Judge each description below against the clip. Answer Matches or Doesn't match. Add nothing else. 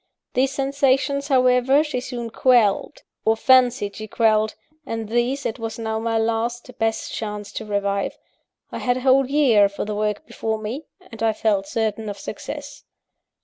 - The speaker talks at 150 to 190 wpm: Matches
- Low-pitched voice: Doesn't match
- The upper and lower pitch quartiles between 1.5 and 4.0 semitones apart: Matches